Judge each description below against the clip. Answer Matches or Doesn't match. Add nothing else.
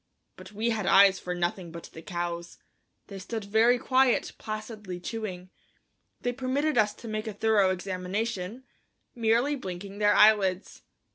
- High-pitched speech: Matches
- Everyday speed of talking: Matches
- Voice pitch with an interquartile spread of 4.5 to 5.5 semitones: Doesn't match